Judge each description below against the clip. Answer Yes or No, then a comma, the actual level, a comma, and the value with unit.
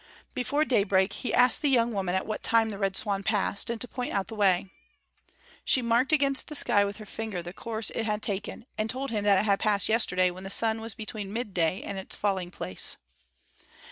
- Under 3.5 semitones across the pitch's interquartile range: Yes, average, 3.0 semitones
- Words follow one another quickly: Yes, fast, 220 wpm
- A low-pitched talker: No, high, 210 Hz